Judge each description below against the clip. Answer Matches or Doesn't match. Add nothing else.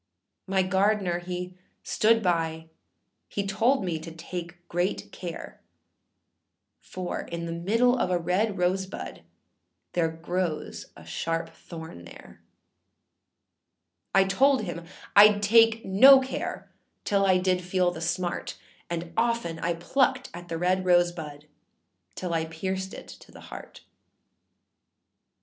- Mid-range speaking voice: Matches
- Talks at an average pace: Doesn't match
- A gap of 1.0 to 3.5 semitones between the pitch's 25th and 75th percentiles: Matches